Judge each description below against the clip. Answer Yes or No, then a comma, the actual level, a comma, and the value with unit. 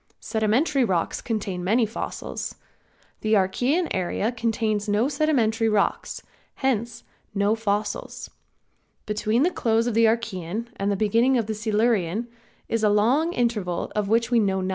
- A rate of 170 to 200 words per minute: No, average, 140 wpm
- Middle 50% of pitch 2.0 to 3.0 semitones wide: Yes, narrow, 2.4 semitones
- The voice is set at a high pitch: Yes, high, 220 Hz